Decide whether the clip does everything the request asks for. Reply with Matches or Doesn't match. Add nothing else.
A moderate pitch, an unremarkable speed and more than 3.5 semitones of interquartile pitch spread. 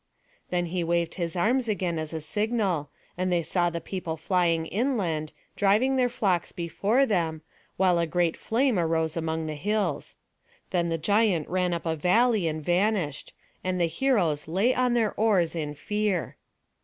Matches